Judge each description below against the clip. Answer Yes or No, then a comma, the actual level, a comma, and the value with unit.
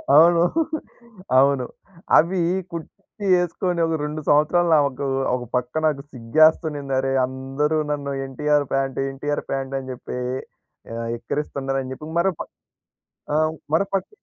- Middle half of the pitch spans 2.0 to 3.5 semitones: Yes, average, 2.9 semitones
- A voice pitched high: No, medium, 145 Hz